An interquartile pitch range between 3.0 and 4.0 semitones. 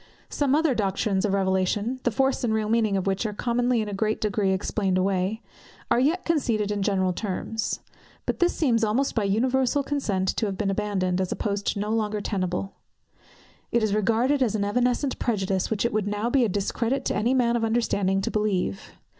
Yes: average, 3.5 semitones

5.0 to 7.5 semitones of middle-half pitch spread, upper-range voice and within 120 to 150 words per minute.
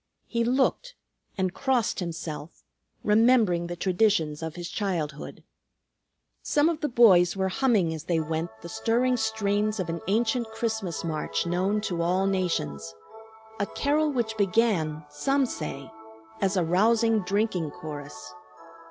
Yes: average, 5.3 semitones; high, 195 Hz; slow, 135 wpm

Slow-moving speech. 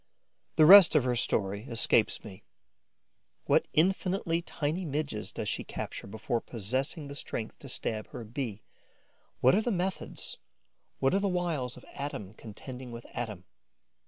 No: average, 145 wpm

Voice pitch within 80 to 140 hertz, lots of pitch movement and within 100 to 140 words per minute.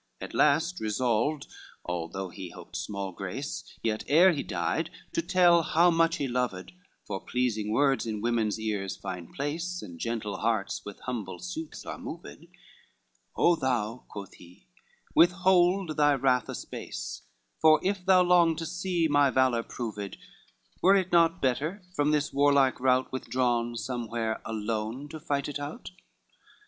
No: low, 135 Hz; wide, 6.9 semitones; average, 155 wpm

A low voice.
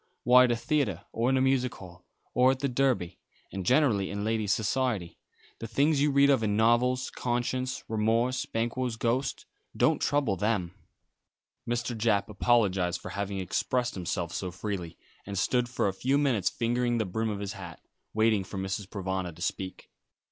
Yes: low, 115 Hz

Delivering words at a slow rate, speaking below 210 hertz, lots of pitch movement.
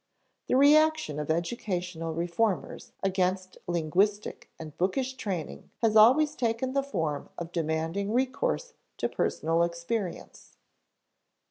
Yes: slow, 110 wpm; high, 190 Hz; wide, 6.7 semitones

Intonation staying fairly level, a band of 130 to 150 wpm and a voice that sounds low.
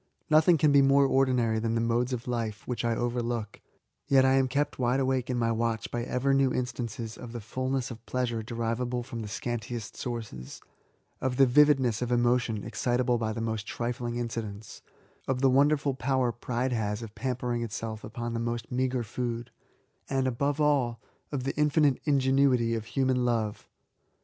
No: narrow, 2.2 semitones; average, 185 wpm; low, 120 Hz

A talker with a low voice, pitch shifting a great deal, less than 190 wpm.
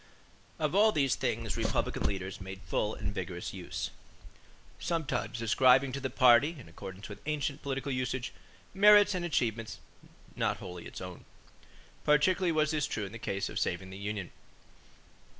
Yes: low, 125 Hz; wide, 7.1 semitones; average, 155 wpm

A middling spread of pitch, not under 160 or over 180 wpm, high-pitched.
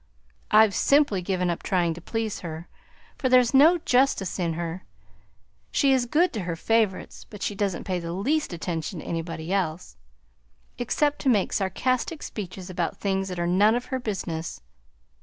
No: wide, 6.0 semitones; average, 170 wpm; high, 195 Hz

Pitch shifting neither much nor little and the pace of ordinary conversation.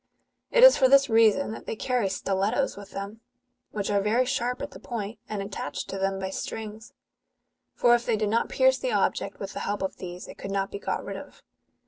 No: average, 3.7 semitones; fast, 220 wpm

